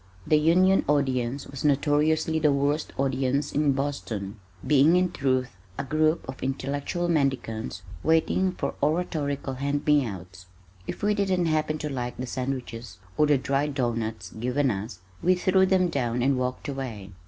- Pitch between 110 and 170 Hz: Yes, medium, 140 Hz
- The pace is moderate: Yes, average, 155 wpm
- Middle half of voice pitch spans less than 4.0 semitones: Yes, average, 3.5 semitones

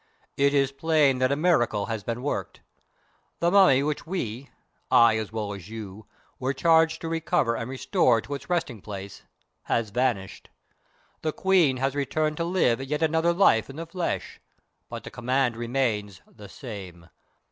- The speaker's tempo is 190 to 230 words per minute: No, average, 165 wpm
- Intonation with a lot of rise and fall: Yes, wide, 6.1 semitones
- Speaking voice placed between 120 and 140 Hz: Yes, low, 135 Hz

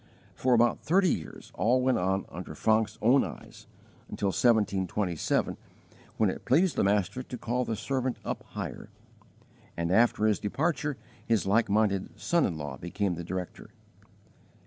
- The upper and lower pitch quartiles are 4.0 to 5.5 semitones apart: Yes, average, 5.0 semitones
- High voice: No, low, 110 Hz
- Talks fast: No, average, 150 wpm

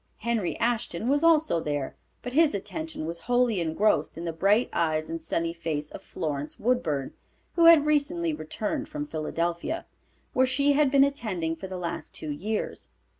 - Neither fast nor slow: Yes, average, 170 wpm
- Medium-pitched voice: No, high, 210 Hz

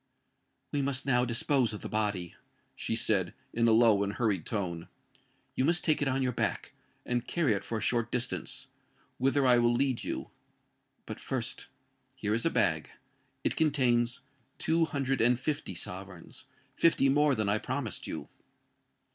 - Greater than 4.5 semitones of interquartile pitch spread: No, average, 4.0 semitones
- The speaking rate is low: No, average, 160 wpm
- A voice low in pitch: Yes, low, 120 Hz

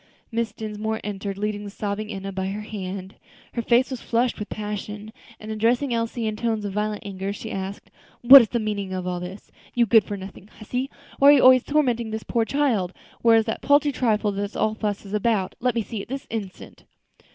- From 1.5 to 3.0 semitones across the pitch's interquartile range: Yes, average, 2.7 semitones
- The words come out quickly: Yes, fast, 220 wpm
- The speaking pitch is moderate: No, high, 215 Hz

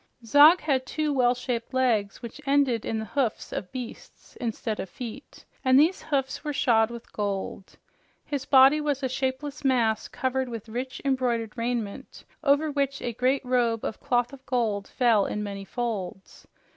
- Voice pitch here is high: Yes, very high, 250 Hz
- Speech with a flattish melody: No, average, 3.4 semitones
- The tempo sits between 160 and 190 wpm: Yes, average, 170 wpm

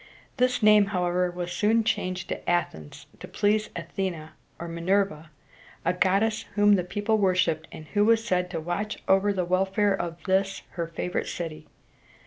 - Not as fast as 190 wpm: Yes, average, 170 wpm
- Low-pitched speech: No, medium, 185 Hz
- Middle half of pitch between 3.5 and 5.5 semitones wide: No, average, 3.0 semitones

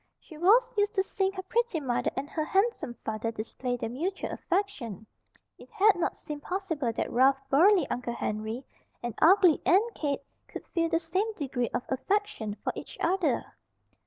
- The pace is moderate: Yes, average, 170 wpm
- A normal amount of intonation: No, wide, 7.7 semitones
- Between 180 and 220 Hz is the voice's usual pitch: No, very high, 325 Hz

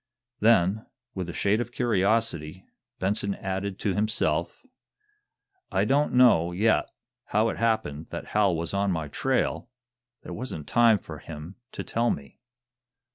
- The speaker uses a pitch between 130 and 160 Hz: No, low, 100 Hz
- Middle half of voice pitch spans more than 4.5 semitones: Yes, average, 5.0 semitones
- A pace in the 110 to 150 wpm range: Yes, average, 140 wpm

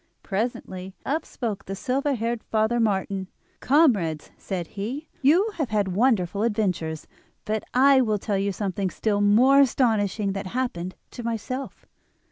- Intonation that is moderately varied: Yes, average, 4.7 semitones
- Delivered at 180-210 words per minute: No, average, 140 wpm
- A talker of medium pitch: No, high, 215 Hz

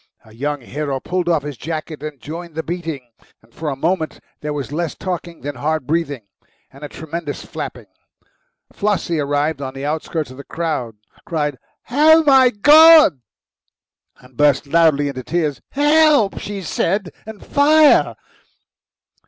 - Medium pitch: Yes, medium, 160 Hz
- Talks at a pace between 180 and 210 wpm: No, average, 145 wpm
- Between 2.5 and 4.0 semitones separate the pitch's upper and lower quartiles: No, average, 4.4 semitones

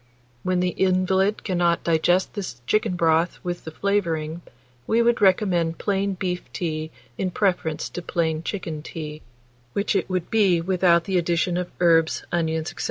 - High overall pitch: No, medium, 175 Hz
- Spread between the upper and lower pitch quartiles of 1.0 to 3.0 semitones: Yes, narrow, 2.6 semitones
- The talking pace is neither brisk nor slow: Yes, average, 160 wpm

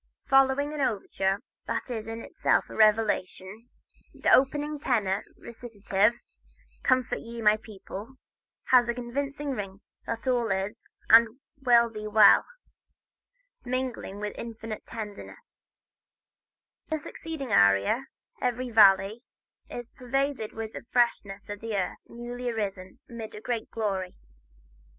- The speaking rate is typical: No, slow, 120 wpm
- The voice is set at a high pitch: Yes, high, 225 Hz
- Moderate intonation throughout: Yes, average, 3.3 semitones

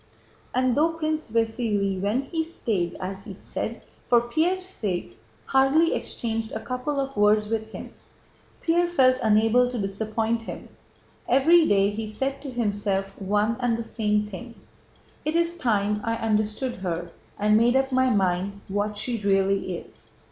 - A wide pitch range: No, average, 4.0 semitones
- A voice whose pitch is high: Yes, high, 225 Hz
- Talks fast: No, average, 160 wpm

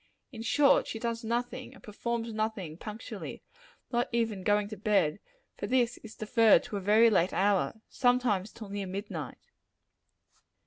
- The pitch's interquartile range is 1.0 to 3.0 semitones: Yes, narrow, 2.6 semitones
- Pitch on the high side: Yes, high, 220 Hz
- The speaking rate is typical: Yes, average, 150 wpm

